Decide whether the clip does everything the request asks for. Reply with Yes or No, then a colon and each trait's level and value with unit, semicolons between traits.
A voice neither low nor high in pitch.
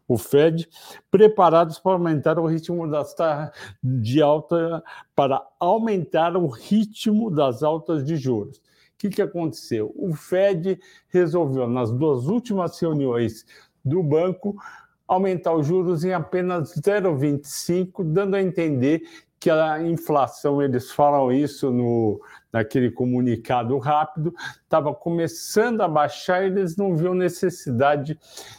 Yes: medium, 165 Hz